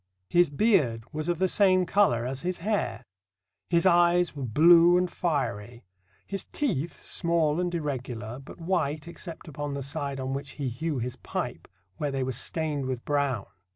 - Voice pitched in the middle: Yes, medium, 150 Hz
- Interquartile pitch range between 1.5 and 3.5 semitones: No, average, 4.8 semitones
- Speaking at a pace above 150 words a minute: Yes, average, 170 wpm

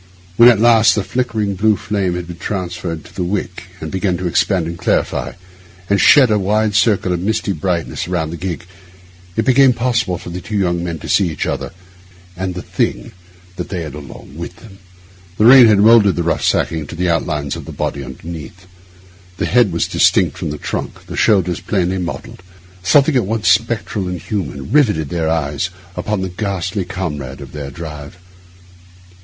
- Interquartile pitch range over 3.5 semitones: Yes, average, 4.0 semitones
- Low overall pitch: Yes, very low, 90 Hz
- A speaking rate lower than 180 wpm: No, average, 185 wpm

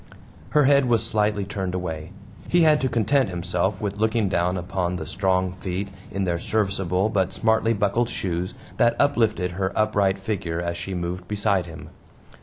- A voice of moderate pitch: No, very low, 95 Hz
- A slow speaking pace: No, average, 170 wpm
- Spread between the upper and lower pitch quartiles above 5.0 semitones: No, average, 3.4 semitones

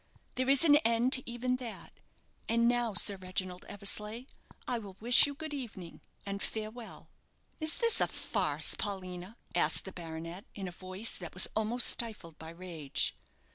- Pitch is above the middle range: Yes, high, 215 Hz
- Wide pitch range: No, average, 4.8 semitones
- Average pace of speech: Yes, average, 165 wpm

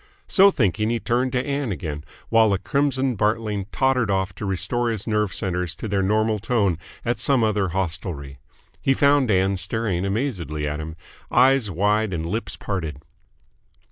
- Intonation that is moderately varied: Yes, average, 4.6 semitones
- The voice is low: Yes, low, 105 Hz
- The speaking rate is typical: Yes, average, 165 wpm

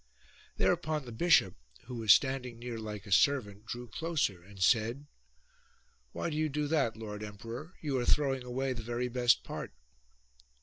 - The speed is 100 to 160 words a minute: No, average, 170 wpm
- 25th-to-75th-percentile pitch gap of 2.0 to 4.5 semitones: Yes, average, 4.2 semitones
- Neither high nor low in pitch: No, low, 120 Hz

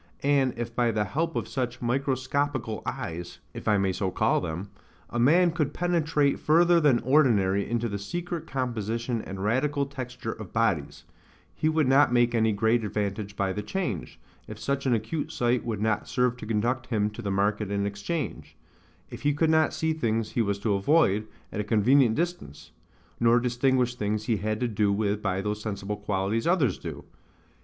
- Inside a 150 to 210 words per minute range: Yes, average, 185 wpm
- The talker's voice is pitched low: Yes, low, 115 Hz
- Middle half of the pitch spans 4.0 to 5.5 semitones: Yes, average, 5.0 semitones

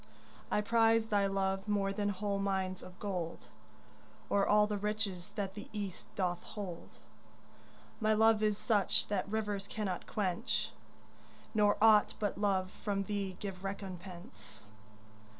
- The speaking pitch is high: Yes, high, 200 Hz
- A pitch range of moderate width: No, narrow, 1.8 semitones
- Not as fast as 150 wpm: Yes, slow, 135 wpm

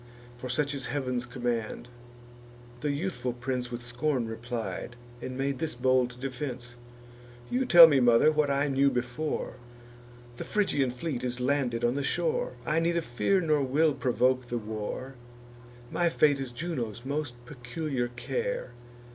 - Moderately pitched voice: No, low, 130 Hz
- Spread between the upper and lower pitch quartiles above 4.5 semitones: No, average, 3.7 semitones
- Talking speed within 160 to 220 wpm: No, average, 145 wpm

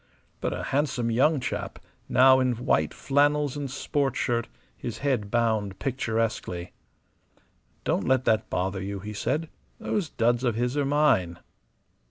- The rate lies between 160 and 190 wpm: No, average, 145 wpm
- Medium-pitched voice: No, low, 120 Hz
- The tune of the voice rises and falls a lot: No, average, 4.2 semitones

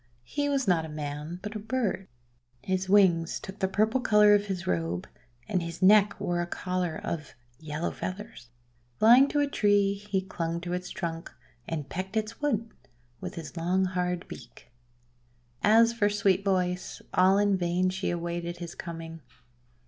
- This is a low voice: No, medium, 185 Hz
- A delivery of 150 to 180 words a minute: Yes, average, 165 wpm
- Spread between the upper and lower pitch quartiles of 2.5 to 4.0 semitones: Yes, average, 3.4 semitones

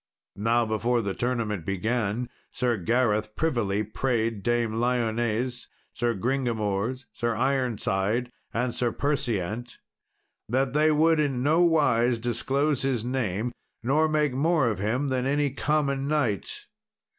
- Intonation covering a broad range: No, average, 3.5 semitones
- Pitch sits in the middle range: No, low, 120 Hz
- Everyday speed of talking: No, slow, 125 wpm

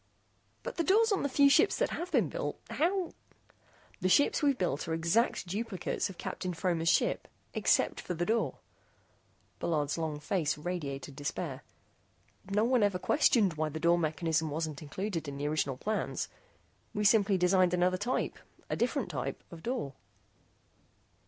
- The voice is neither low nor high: Yes, medium, 180 Hz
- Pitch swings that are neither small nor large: No, wide, 6.4 semitones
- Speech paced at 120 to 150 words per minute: No, average, 160 wpm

